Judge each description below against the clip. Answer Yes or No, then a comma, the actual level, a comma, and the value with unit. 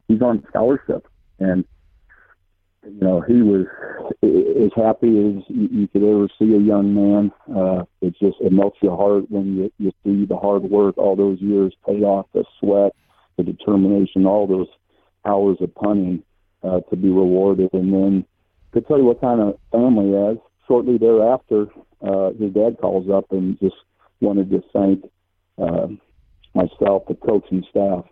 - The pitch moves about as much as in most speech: No, narrow, 1.7 semitones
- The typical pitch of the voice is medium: No, low, 100 Hz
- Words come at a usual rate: Yes, average, 165 wpm